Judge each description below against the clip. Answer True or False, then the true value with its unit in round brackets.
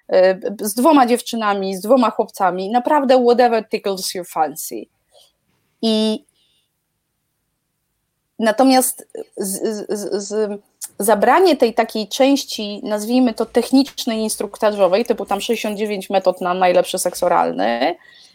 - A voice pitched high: True (220 Hz)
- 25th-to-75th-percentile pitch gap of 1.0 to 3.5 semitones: False (3.9 semitones)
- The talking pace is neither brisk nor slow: False (105 wpm)